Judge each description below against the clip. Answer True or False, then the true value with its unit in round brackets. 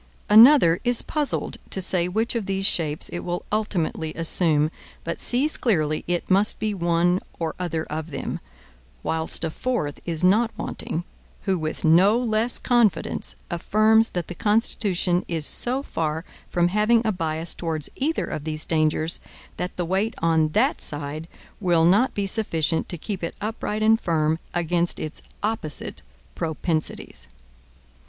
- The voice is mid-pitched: True (175 Hz)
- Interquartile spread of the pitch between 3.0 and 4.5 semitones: False (5.0 semitones)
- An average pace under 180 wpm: True (150 wpm)